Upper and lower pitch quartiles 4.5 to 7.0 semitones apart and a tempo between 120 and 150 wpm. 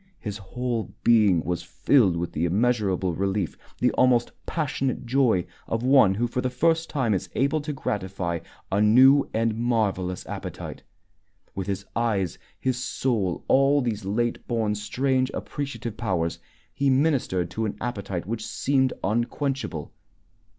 Yes: average, 5.0 semitones; average, 145 wpm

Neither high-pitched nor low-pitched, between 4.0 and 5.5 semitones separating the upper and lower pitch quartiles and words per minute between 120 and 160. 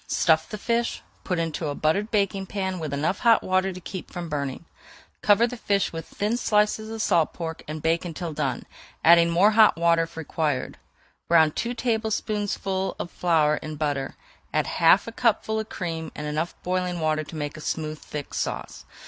No: medium, 170 Hz; average, 4.7 semitones; average, 185 wpm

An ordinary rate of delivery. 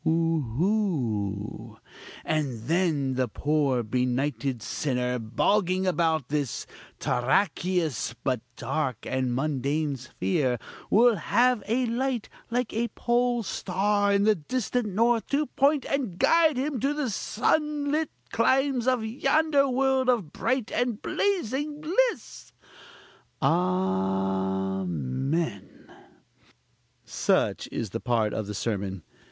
No: slow, 110 wpm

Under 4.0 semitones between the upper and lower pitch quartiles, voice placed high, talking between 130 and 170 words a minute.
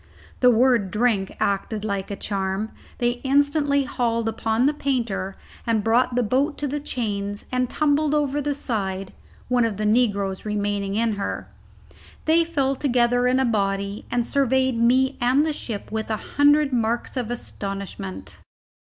No: average, 4.4 semitones; high, 235 Hz; average, 160 wpm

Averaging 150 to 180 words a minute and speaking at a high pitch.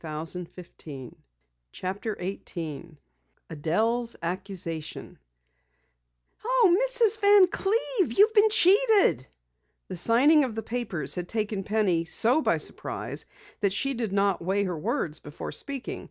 No: average, 140 wpm; high, 210 Hz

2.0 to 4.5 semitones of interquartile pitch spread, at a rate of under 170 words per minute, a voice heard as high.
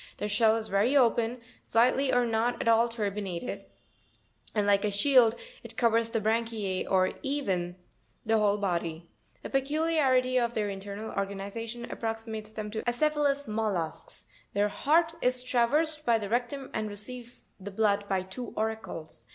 Yes: average, 3.5 semitones; average, 160 wpm; high, 225 Hz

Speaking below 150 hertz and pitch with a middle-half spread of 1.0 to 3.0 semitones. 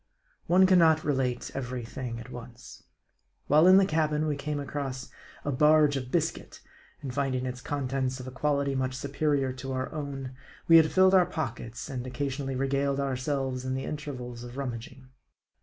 Yes: low, 135 Hz; narrow, 2.6 semitones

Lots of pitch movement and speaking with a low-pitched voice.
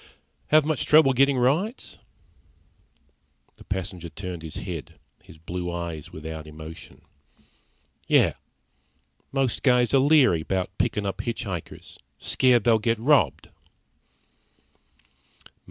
Yes: wide, 7.8 semitones; low, 105 Hz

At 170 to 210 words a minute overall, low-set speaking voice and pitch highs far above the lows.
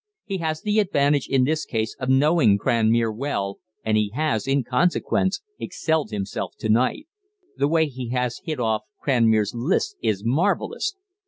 No: average, 160 wpm; low, 130 Hz; wide, 6.0 semitones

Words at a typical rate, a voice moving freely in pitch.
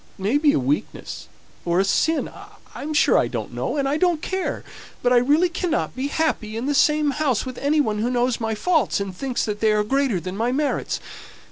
No: fast, 225 wpm; wide, 5.9 semitones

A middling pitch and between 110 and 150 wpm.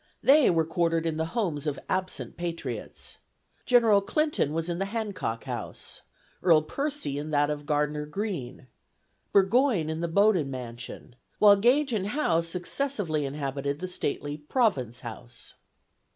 Yes: medium, 165 Hz; average, 140 wpm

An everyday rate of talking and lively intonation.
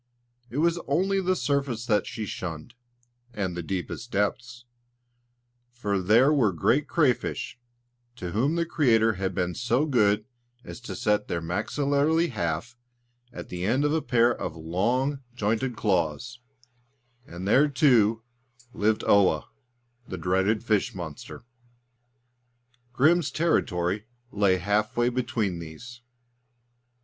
No: slow, 125 wpm; wide, 5.7 semitones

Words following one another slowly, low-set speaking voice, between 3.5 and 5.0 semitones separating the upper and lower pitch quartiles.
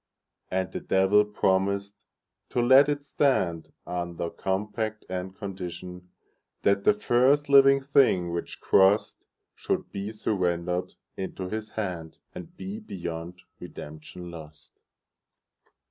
Yes: slow, 100 wpm; very low, 95 Hz; average, 4.1 semitones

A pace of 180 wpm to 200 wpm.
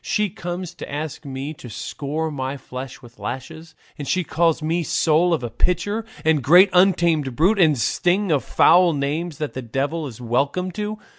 Yes: average, 190 wpm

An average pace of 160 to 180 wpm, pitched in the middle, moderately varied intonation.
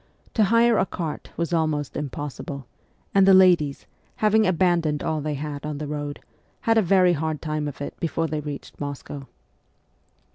Yes: average, 170 wpm; medium, 155 Hz; average, 3.9 semitones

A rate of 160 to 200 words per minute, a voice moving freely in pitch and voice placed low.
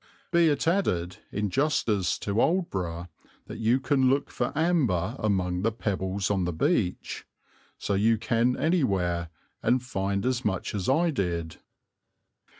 No: average, 145 wpm; wide, 6.2 semitones; low, 105 Hz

